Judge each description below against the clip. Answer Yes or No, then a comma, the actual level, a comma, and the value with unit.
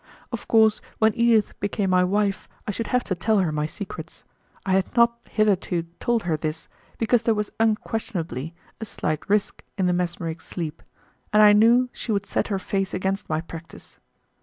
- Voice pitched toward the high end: Yes, high, 200 Hz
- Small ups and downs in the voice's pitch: No, average, 4.1 semitones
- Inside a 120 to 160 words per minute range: No, average, 185 wpm